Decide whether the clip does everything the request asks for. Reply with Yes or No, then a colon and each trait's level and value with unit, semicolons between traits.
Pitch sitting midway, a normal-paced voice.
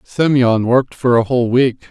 No: low, 125 Hz; average, 190 wpm